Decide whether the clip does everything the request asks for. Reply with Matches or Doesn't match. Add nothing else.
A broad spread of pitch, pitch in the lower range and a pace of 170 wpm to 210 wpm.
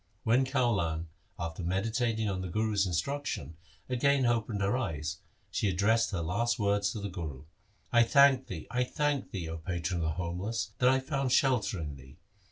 Matches